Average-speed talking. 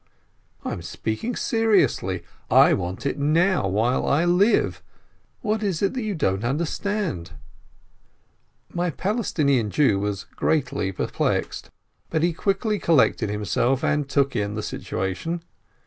No: slow, 130 wpm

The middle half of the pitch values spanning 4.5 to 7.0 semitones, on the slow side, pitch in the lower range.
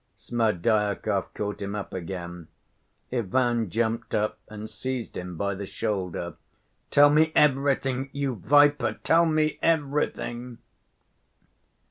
Yes: wide, 5.4 semitones; slow, 110 wpm; low, 115 Hz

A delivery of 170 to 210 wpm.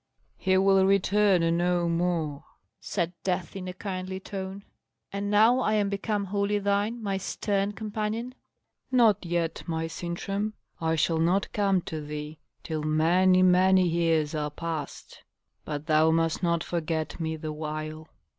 No: average, 145 wpm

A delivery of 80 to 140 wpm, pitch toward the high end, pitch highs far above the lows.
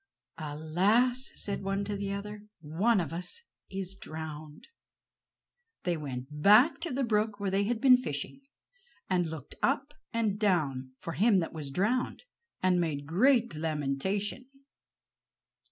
Yes: slow, 135 wpm; high, 195 Hz; wide, 5.8 semitones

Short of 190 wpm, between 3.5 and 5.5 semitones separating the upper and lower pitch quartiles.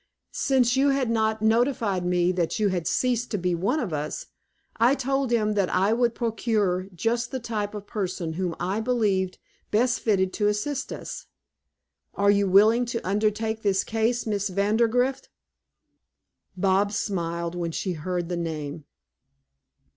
Yes: average, 155 wpm; average, 4.3 semitones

